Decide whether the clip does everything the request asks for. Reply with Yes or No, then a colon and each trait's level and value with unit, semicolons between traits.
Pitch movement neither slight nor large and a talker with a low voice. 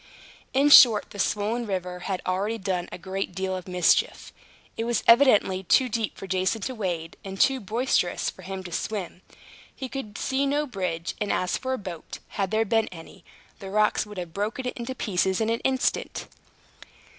No: average, 4.0 semitones; high, 205 Hz